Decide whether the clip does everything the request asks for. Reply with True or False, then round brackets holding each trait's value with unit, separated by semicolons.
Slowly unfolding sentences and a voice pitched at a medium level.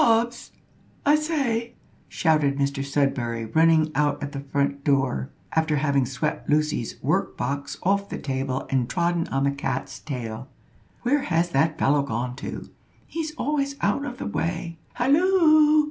False (150 wpm; 150 Hz)